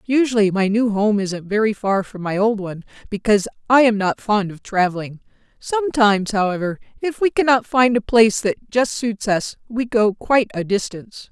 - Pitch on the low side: No, high, 215 Hz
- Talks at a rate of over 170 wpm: Yes, average, 185 wpm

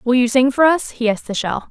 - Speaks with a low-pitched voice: No, high, 245 Hz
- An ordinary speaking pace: No, fast, 315 wpm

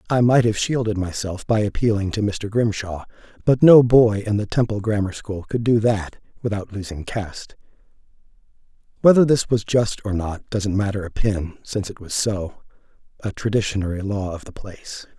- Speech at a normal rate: Yes, average, 170 wpm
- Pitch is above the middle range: No, low, 105 Hz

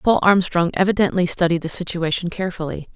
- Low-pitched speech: No, medium, 175 Hz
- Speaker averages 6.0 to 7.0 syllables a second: Yes, 6.1 syllables/s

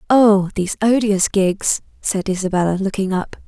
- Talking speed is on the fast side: No, average, 140 wpm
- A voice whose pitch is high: Yes, high, 200 Hz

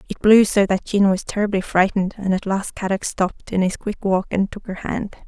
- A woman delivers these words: Yes, female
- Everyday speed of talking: No, fast, 240 wpm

